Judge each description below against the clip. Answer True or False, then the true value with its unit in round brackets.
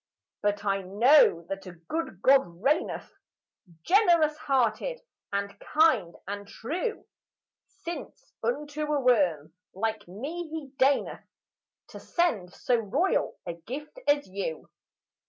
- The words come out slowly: True (120 wpm)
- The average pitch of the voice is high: True (250 Hz)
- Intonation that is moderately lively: False (7.7 semitones)